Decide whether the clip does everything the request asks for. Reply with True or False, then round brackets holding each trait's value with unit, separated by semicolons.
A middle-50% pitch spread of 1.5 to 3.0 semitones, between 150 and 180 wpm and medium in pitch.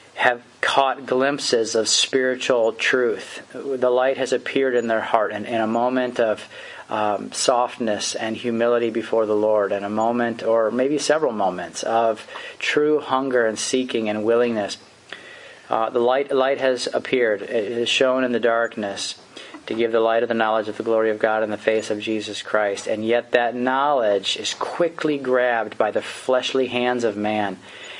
False (2.6 semitones; 175 wpm; 115 Hz)